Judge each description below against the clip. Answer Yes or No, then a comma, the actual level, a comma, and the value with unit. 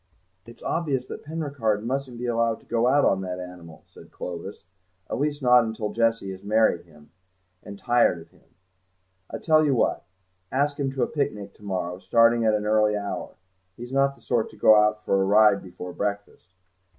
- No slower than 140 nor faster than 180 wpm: No, average, 195 wpm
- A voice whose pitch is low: Yes, low, 110 Hz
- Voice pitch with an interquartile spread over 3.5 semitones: Yes, average, 4.4 semitones